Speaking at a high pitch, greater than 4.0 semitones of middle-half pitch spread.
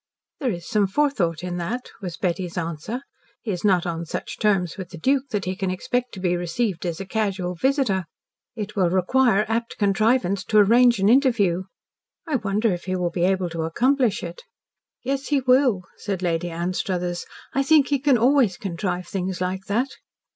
Yes: high, 195 Hz; wide, 5.4 semitones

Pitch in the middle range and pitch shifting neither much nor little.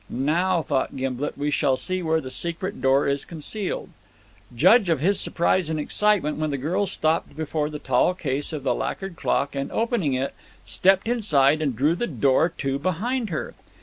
Yes: medium, 155 Hz; average, 4.9 semitones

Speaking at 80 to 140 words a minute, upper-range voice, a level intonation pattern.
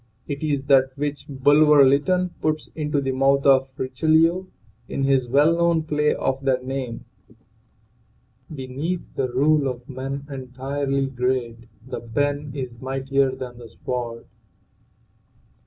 No: slow, 135 wpm; low, 135 Hz; narrow, 2.2 semitones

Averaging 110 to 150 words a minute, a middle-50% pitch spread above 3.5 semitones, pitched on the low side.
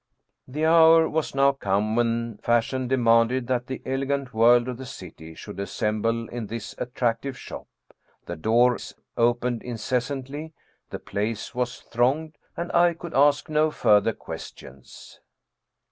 No: average, 145 wpm; average, 3.2 semitones; low, 125 Hz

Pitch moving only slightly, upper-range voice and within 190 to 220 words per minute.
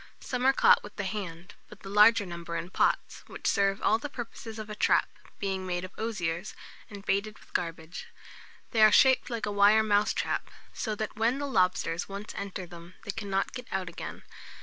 No: average, 3.0 semitones; high, 205 Hz; average, 195 wpm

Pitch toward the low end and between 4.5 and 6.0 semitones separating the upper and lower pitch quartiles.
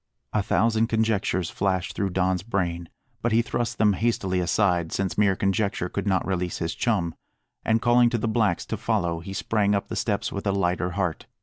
No: low, 100 Hz; average, 3.5 semitones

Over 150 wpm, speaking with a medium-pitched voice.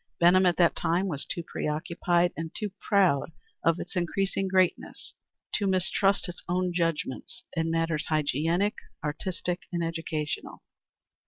No: slow, 135 wpm; medium, 175 Hz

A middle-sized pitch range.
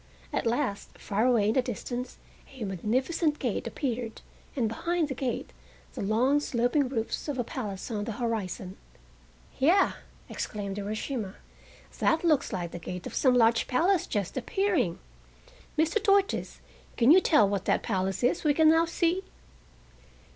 No: wide, 6.2 semitones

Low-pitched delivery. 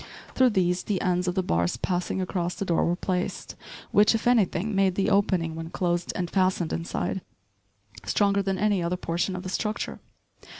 No: medium, 185 Hz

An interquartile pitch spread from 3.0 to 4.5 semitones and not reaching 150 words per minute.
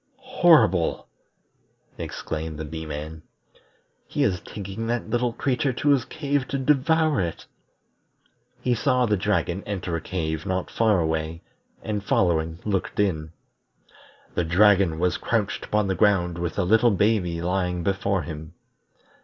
No: wide, 5.4 semitones; average, 140 wpm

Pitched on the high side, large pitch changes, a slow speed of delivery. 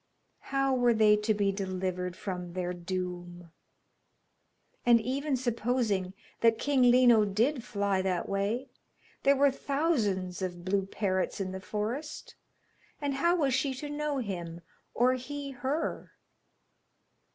Yes: high, 220 Hz; wide, 6.1 semitones; slow, 130 wpm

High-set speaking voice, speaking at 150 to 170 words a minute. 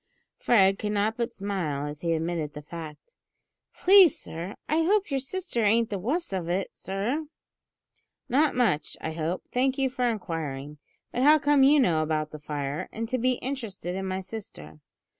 No: high, 200 Hz; average, 180 wpm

